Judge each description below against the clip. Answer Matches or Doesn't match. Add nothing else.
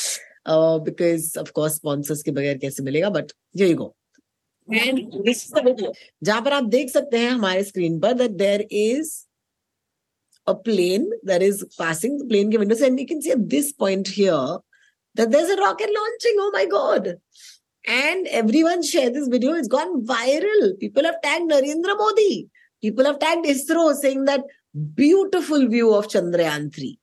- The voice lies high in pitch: Matches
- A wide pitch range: Matches